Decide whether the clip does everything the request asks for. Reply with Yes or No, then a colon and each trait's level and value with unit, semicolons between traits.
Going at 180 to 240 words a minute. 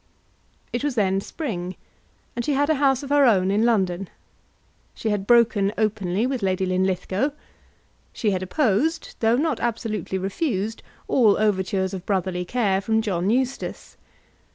No: average, 150 wpm